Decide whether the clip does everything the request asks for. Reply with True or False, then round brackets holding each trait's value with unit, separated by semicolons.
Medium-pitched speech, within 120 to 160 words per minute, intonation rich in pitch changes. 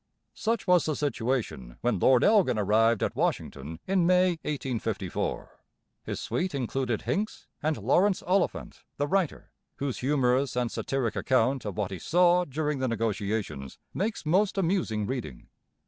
False (130 Hz; 145 wpm; 7.8 semitones)